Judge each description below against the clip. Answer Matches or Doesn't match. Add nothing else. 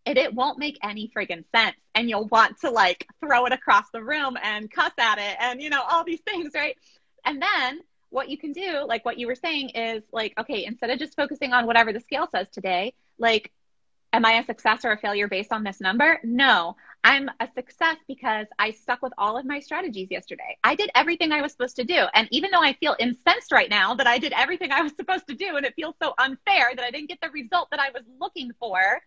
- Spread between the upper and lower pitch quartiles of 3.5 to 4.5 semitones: Doesn't match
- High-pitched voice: Matches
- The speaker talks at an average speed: Doesn't match